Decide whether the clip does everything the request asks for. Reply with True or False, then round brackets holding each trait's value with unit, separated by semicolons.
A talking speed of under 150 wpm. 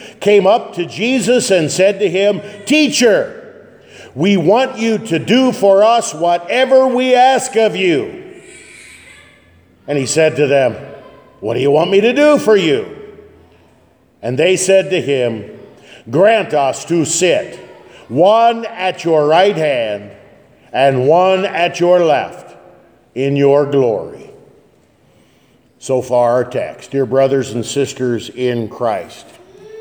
True (135 wpm)